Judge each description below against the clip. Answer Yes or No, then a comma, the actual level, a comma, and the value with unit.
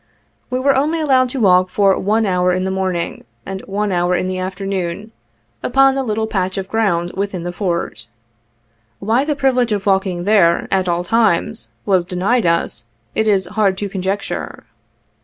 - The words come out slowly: No, average, 175 wpm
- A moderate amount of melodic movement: Yes, average, 3.4 semitones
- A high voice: Yes, high, 195 Hz